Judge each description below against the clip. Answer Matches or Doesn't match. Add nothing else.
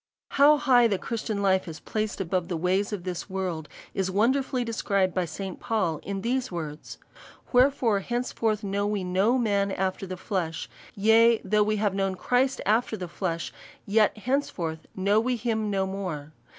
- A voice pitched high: Matches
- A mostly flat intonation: Doesn't match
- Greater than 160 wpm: Matches